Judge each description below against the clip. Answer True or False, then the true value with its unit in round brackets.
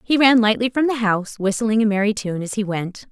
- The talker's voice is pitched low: False (220 Hz)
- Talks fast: True (250 wpm)